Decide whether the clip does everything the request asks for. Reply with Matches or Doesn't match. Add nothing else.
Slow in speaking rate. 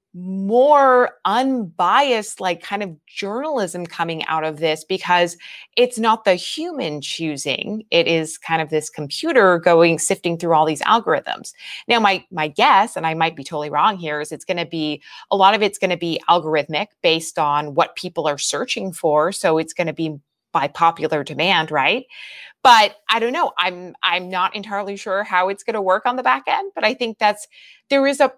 Doesn't match